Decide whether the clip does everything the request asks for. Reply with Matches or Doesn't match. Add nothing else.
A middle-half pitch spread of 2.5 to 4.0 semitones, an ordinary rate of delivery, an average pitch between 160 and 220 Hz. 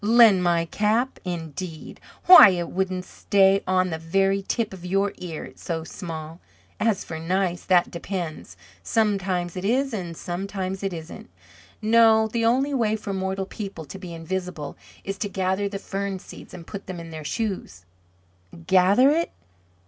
Matches